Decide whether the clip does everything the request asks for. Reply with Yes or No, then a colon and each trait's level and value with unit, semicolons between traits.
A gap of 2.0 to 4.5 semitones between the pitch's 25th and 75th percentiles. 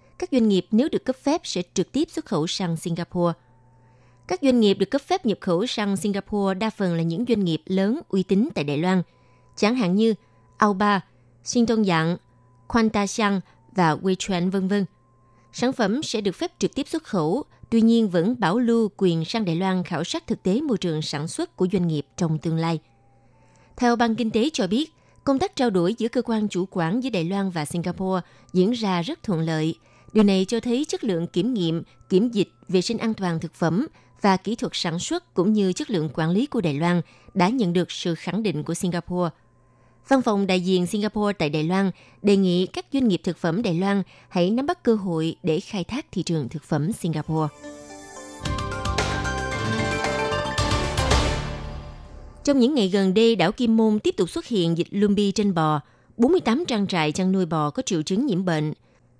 No: wide, 5.4 semitones